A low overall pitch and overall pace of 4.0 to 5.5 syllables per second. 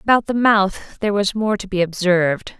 No: high, 200 Hz; 5.1 syllables/s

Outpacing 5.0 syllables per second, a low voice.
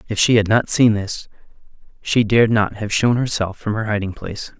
Yes: 5.5 syllables/s; low, 110 Hz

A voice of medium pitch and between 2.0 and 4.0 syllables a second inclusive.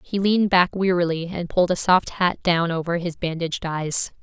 No: medium, 175 Hz; 5.2 syllables/s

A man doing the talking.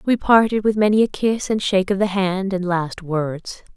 No: female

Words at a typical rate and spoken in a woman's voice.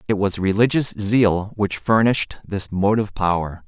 No: average, 145 wpm; male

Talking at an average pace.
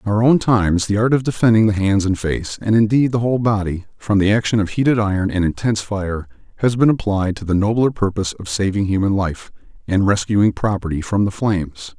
No: fast, 215 wpm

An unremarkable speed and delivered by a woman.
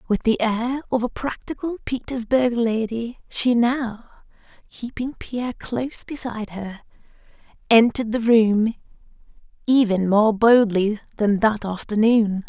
No: slow, 115 wpm; female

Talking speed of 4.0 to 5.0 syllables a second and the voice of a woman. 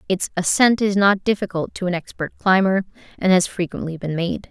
No: 5.4 syllables/s; female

